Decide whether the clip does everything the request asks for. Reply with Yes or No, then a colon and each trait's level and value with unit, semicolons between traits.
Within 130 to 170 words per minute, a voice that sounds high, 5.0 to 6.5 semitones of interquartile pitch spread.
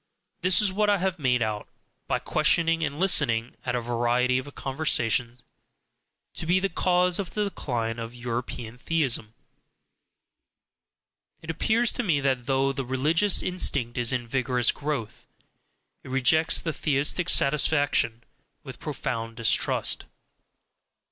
No: slow, 135 wpm; low, 135 Hz; wide, 5.4 semitones